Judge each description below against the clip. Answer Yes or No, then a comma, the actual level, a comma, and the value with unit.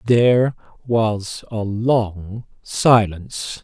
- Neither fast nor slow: No, slow, 80 wpm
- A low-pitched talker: Yes, low, 110 Hz